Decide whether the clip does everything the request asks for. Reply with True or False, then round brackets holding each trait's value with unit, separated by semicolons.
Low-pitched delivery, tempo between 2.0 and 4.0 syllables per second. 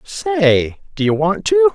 True (125 Hz; 3.9 syllables/s)